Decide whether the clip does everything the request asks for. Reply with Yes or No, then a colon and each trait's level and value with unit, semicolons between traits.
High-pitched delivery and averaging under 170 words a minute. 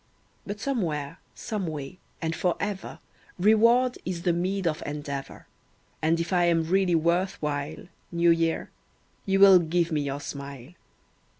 No: medium, 170 Hz; average, 145 wpm